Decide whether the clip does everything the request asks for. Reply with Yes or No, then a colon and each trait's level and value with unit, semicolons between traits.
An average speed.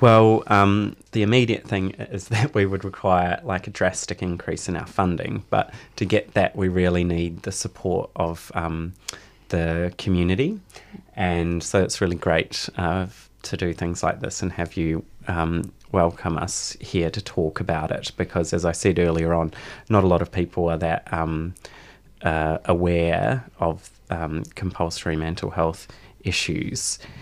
Yes: average, 165 wpm